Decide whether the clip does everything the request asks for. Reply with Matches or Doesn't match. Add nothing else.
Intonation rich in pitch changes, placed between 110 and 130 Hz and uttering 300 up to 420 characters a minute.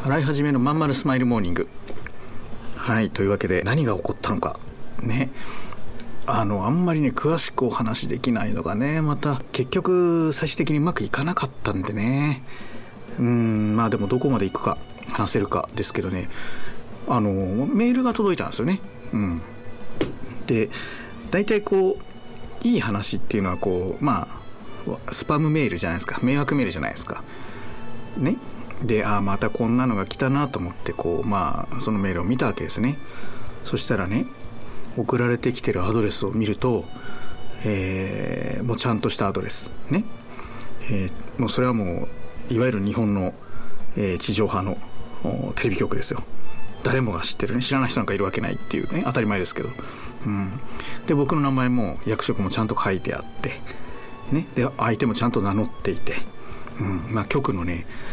Doesn't match